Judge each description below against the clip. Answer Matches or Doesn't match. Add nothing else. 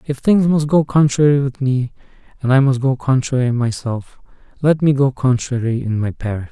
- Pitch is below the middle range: Matches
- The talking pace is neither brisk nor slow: Matches